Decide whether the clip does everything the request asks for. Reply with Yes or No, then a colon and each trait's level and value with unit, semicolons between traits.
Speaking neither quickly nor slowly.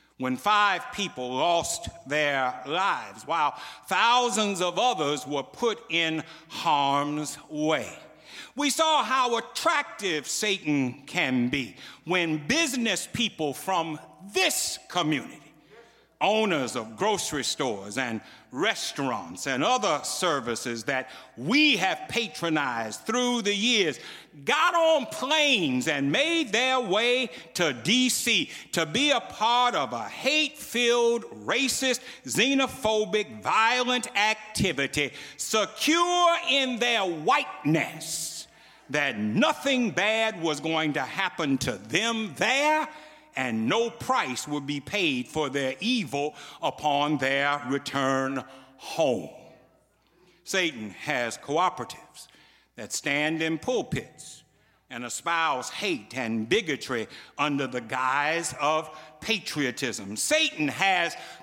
No: slow, 110 wpm